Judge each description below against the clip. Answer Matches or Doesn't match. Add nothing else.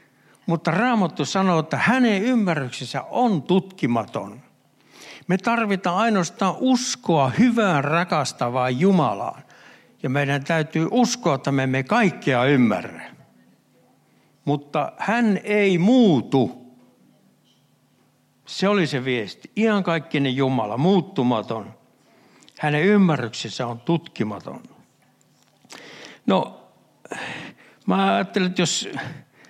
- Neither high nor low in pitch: Matches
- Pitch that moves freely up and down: Matches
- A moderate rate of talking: Doesn't match